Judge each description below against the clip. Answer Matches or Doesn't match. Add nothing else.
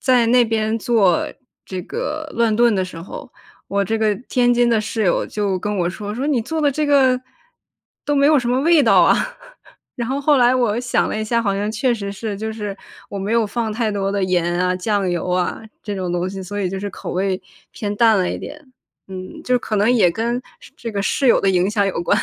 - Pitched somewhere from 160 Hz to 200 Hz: Doesn't match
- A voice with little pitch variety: Doesn't match